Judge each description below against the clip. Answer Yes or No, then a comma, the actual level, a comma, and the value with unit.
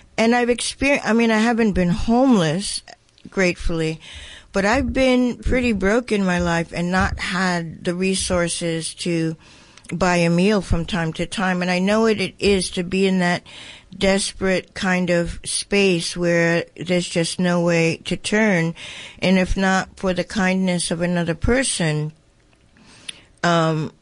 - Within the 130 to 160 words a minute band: Yes, average, 155 wpm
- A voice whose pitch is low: No, medium, 180 Hz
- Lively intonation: No, average, 2.8 semitones